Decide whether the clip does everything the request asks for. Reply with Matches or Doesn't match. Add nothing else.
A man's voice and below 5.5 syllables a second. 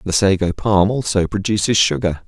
Matches